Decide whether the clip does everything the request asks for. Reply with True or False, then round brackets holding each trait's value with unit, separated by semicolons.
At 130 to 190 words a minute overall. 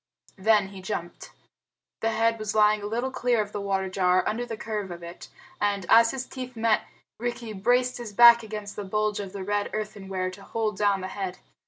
False (205 wpm)